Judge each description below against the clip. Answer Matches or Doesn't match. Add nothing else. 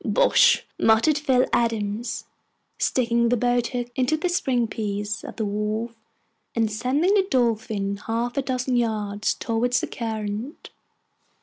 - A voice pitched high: Matches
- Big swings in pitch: Doesn't match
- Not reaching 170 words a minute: Matches